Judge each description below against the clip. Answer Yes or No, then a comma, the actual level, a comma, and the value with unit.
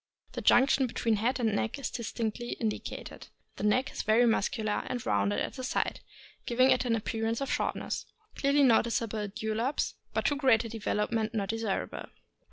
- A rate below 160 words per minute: No, average, 175 wpm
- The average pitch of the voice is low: No, high, 230 Hz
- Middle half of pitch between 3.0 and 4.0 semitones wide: No, narrow, 2.6 semitones